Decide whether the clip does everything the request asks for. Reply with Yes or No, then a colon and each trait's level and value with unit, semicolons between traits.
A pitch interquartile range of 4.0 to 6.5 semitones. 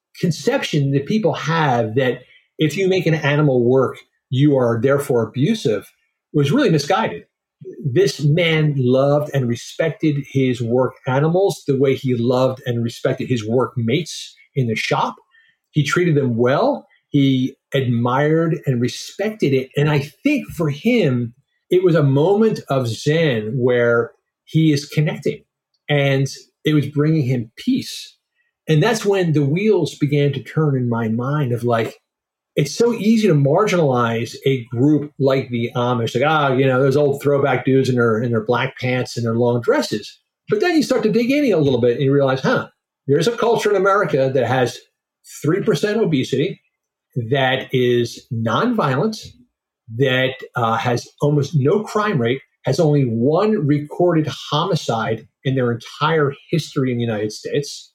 Yes: average, 4.3 semitones